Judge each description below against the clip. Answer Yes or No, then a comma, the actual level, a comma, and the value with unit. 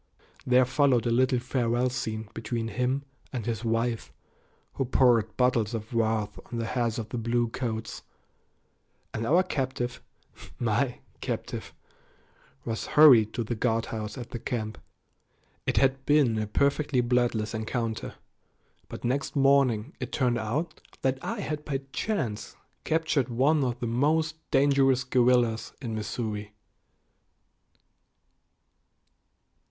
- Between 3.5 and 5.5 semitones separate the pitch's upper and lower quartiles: No, average, 2.9 semitones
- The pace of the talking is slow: Yes, slow, 125 wpm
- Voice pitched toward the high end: No, low, 120 Hz